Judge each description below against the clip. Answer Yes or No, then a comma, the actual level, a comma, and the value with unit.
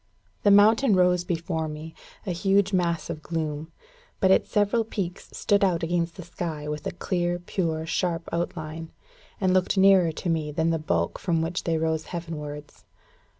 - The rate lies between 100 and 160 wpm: No, average, 175 wpm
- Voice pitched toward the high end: No, medium, 170 Hz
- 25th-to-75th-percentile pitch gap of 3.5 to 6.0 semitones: No, narrow, 2.6 semitones